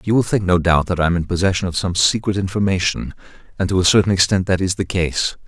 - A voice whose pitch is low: Yes, very low, 95 Hz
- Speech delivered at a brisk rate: Yes, fast, 250 wpm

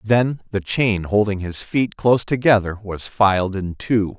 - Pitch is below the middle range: Yes, low, 105 Hz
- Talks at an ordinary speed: Yes, average, 170 wpm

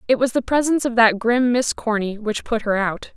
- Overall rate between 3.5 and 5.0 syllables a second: No, 5.4 syllables/s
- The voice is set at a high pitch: Yes, high, 230 Hz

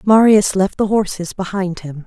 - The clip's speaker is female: Yes, female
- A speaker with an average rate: Yes, average, 175 wpm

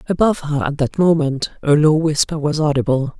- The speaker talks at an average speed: Yes, average, 190 wpm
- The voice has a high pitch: No, medium, 150 Hz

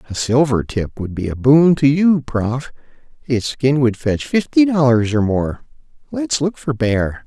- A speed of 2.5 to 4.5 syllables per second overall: Yes, 4.1 syllables/s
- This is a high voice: No, low, 130 Hz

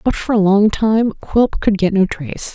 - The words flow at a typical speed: No, fast, 235 wpm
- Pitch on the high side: Yes, high, 205 Hz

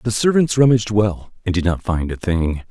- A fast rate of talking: Yes, fast, 220 wpm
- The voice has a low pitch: Yes, low, 105 Hz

